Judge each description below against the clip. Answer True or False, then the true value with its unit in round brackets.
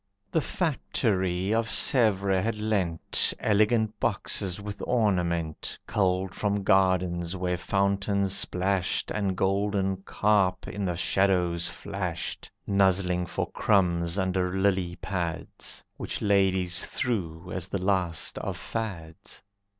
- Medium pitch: False (95 Hz)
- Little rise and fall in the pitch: True (2.2 semitones)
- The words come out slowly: True (110 wpm)